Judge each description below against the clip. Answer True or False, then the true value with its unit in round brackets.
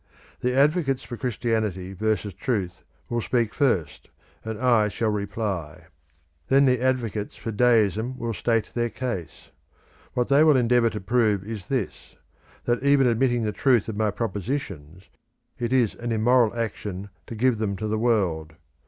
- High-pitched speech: False (115 Hz)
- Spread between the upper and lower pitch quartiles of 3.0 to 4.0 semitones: True (3.3 semitones)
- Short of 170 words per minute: True (160 wpm)